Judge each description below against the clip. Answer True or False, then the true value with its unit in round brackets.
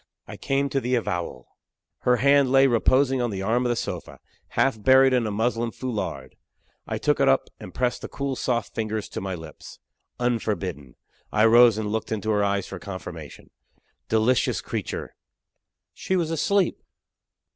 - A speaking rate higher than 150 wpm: True (170 wpm)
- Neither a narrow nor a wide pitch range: True (4.3 semitones)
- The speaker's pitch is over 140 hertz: False (115 Hz)